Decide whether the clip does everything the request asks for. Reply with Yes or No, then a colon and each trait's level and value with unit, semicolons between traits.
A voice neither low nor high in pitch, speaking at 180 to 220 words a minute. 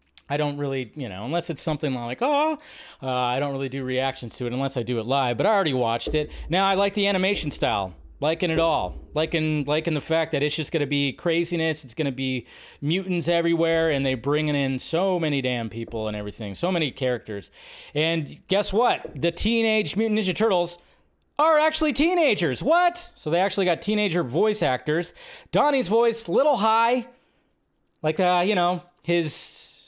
Yes: medium, 165 Hz; average, 190 wpm